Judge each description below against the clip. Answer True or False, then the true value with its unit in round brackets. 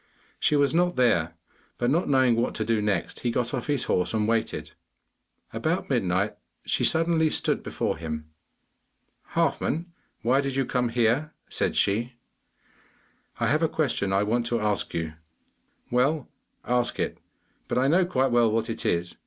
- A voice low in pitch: True (120 Hz)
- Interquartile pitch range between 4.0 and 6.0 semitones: True (4.7 semitones)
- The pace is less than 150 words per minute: False (165 wpm)